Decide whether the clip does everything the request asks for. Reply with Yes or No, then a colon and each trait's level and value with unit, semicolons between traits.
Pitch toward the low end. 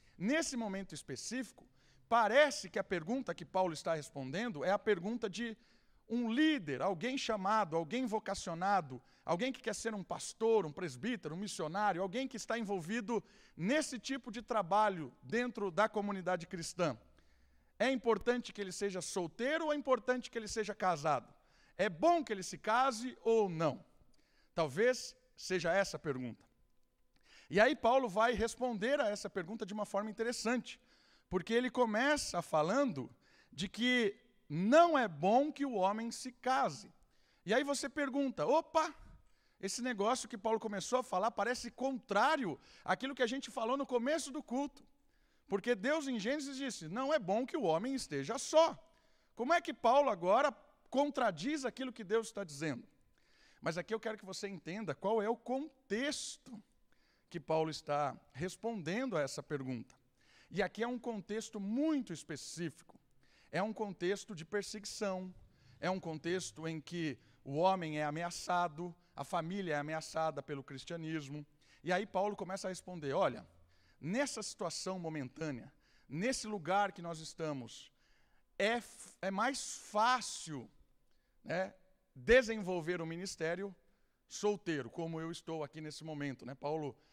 No: high, 205 Hz